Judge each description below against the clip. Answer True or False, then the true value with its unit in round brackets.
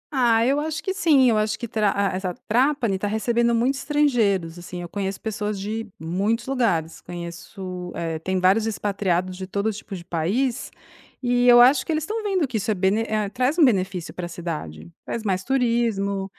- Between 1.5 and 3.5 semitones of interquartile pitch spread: False (4.9 semitones)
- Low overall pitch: False (210 Hz)